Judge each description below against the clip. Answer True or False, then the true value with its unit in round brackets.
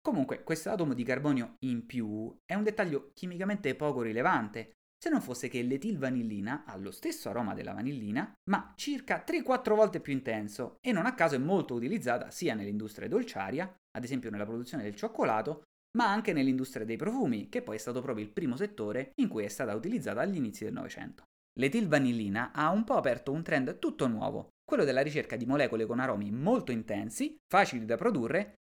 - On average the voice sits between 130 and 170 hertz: True (135 Hz)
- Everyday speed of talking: False (185 wpm)